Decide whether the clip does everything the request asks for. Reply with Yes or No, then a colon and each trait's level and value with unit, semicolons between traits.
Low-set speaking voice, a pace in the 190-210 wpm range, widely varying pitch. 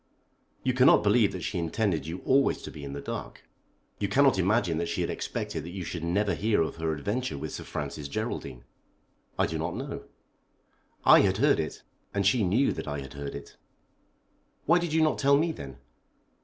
Yes: very low, 95 Hz; average, 200 wpm; wide, 7.9 semitones